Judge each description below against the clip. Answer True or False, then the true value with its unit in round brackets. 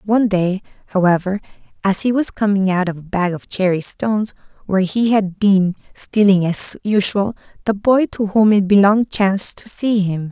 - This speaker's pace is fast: False (180 wpm)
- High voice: True (200 Hz)